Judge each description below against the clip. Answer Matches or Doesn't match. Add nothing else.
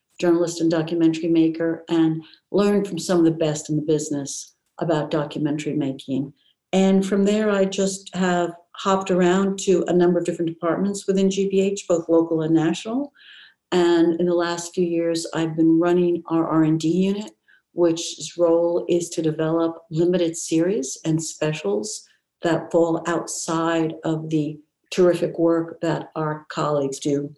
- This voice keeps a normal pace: Matches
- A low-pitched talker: Doesn't match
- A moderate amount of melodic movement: Doesn't match